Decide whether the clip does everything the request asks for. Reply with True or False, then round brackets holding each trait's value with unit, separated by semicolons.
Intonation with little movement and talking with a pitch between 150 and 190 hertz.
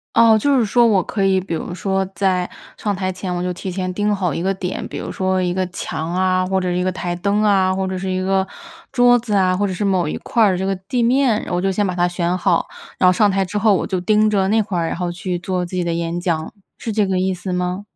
True (2.1 semitones; 185 Hz)